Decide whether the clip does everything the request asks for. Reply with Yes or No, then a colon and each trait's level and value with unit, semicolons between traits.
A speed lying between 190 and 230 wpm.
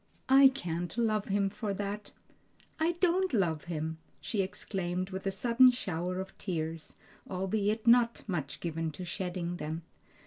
No: average, 145 wpm